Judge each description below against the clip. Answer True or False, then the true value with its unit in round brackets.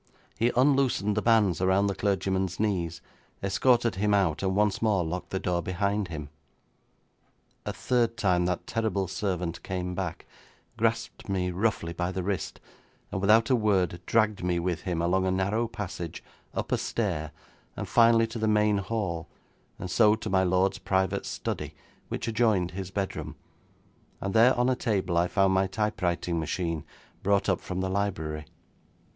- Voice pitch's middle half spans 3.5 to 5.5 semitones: False (3.1 semitones)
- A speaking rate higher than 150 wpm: True (165 wpm)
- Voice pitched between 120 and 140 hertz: False (95 Hz)